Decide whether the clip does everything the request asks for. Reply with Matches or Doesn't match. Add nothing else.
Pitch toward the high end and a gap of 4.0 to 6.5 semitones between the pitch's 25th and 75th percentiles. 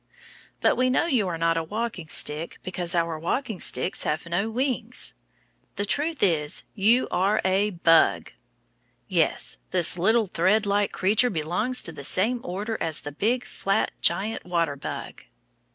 Matches